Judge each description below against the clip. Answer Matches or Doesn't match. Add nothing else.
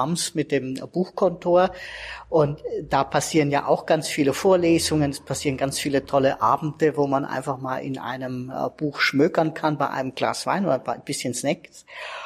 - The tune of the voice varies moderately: Matches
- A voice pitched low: Doesn't match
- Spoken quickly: Doesn't match